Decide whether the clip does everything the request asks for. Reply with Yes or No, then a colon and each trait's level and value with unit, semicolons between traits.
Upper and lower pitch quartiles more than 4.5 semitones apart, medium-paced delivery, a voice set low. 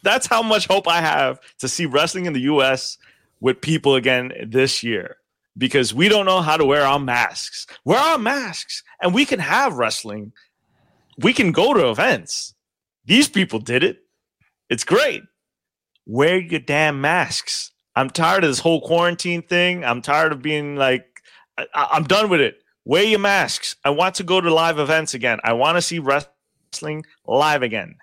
No: average, 5.2 semitones; average, 180 wpm; medium, 155 Hz